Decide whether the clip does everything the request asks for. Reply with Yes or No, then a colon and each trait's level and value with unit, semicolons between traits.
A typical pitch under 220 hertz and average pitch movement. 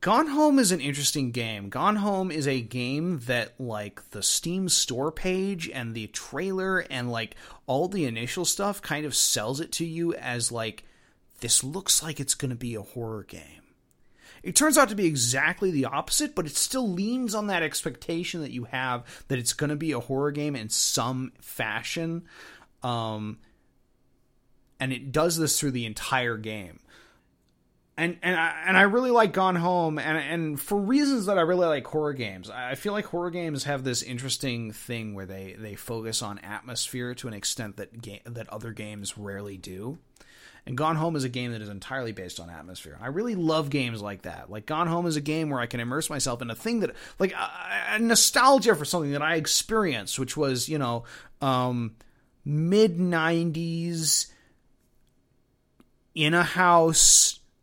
No: medium, 140 Hz; wide, 6.4 semitones